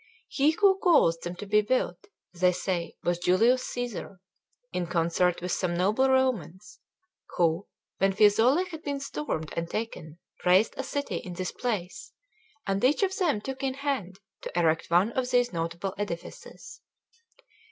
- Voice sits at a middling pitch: No, high, 200 Hz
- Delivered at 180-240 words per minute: No, average, 150 wpm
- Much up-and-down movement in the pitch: Yes, wide, 6.9 semitones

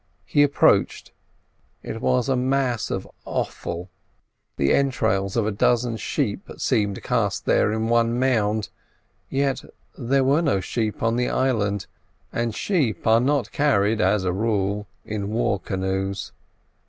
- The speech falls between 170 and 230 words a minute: No, average, 140 wpm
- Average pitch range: Yes, average, 4.0 semitones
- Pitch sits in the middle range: No, low, 115 Hz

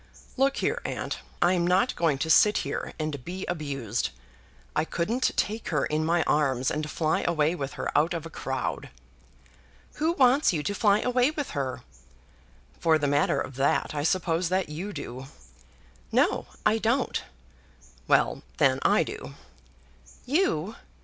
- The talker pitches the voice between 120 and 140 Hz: No, medium, 165 Hz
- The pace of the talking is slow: No, average, 155 wpm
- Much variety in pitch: Yes, wide, 6.0 semitones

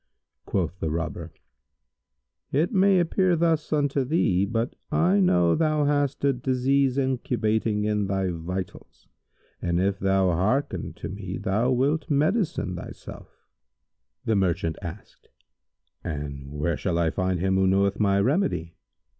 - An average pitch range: No, wide, 7.7 semitones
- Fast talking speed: No, slow, 135 wpm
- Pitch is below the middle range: Yes, low, 105 Hz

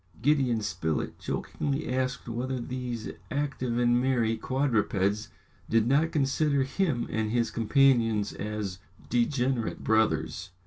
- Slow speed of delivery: Yes, slow, 115 wpm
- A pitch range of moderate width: Yes, average, 3.3 semitones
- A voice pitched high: No, low, 120 Hz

